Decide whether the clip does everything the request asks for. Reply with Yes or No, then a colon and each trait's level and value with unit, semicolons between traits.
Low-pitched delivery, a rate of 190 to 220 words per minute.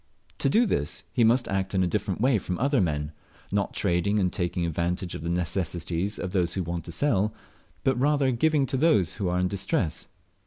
Yes: very low, 95 Hz; fast, 205 wpm